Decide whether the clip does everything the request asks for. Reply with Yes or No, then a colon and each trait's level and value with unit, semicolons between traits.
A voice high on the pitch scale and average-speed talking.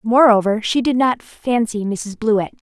Yes: high, 225 Hz; average, 175 wpm